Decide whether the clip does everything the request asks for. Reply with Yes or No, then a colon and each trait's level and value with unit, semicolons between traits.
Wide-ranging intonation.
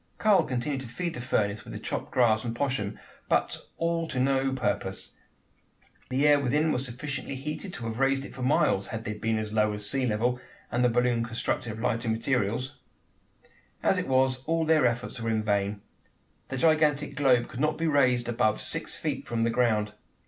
No: average, 3.7 semitones